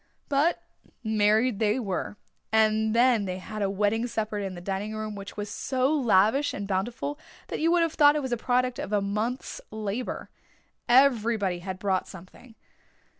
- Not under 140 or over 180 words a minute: Yes, average, 175 wpm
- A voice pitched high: Yes, high, 215 Hz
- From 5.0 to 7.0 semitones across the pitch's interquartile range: No, average, 3.9 semitones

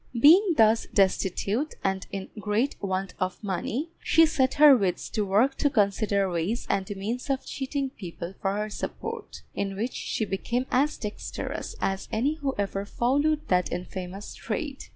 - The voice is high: Yes, high, 215 Hz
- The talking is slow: No, average, 160 wpm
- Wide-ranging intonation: Yes, wide, 5.7 semitones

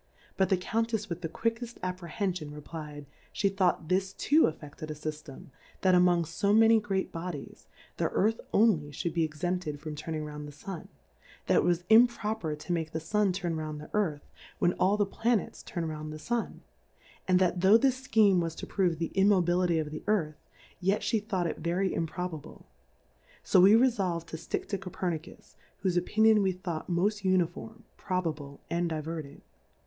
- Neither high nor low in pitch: Yes, medium, 180 Hz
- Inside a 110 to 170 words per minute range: No, average, 180 wpm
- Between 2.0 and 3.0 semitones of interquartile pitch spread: No, average, 4.2 semitones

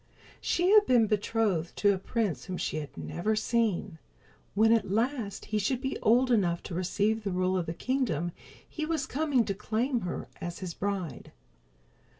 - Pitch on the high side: Yes, high, 210 Hz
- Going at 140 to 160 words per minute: No, average, 175 wpm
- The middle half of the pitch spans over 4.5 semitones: Yes, average, 4.9 semitones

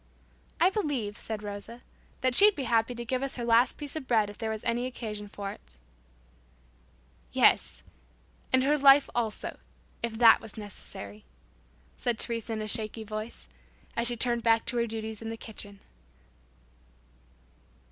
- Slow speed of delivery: No, average, 155 wpm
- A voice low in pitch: No, high, 230 Hz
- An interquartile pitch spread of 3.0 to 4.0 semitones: No, narrow, 2.4 semitones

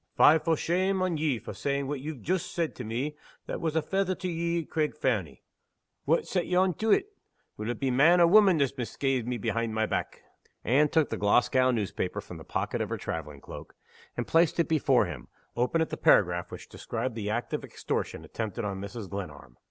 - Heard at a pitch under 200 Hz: Yes, low, 135 Hz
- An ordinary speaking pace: No, fast, 215 wpm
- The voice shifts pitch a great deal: Yes, wide, 7.0 semitones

